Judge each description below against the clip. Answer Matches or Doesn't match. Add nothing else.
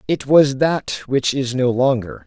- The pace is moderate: Matches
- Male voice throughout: Matches